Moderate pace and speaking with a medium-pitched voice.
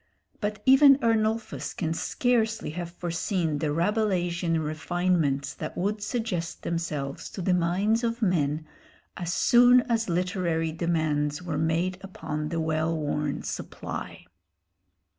No: slow, 120 wpm; medium, 175 Hz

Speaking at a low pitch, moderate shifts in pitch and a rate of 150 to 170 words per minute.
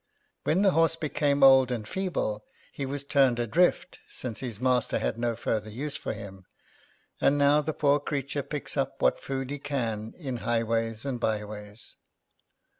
Yes: low, 130 Hz; average, 4.1 semitones; average, 165 wpm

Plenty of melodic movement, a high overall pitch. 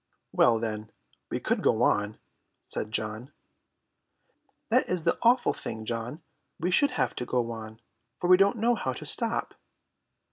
No: wide, 8.7 semitones; low, 125 Hz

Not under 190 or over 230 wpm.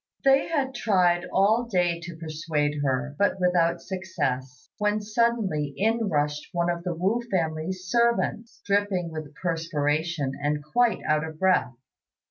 No: average, 140 wpm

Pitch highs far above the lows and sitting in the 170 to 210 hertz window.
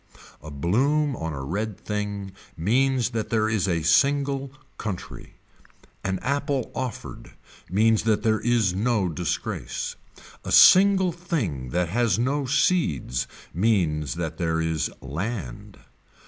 No: wide, 7.8 semitones; low, 105 Hz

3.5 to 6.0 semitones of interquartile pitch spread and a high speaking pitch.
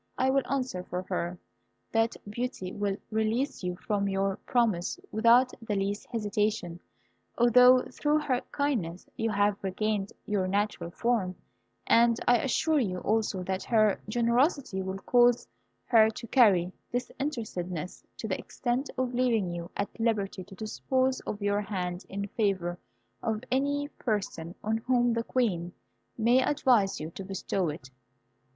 Yes: average, 4.2 semitones; high, 215 Hz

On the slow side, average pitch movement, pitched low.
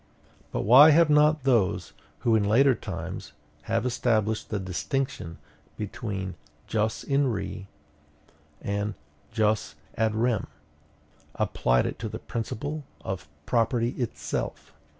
Yes: slow, 115 wpm; average, 4.2 semitones; low, 110 Hz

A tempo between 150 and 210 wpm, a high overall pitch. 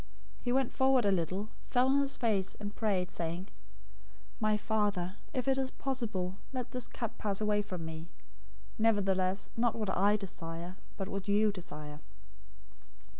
Yes: average, 160 wpm; high, 205 Hz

